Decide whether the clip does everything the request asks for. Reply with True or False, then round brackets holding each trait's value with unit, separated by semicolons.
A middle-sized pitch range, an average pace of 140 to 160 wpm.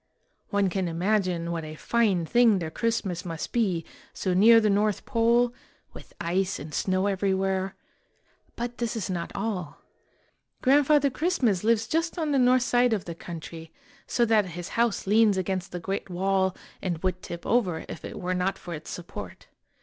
False (4.6 semitones; 175 wpm)